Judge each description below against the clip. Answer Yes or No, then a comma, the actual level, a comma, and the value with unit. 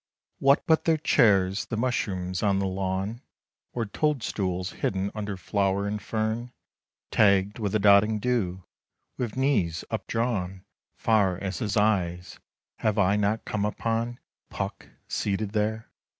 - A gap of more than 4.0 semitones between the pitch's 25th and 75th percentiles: No, average, 2.8 semitones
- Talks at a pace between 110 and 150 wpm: Yes, slow, 135 wpm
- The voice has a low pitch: Yes, low, 105 Hz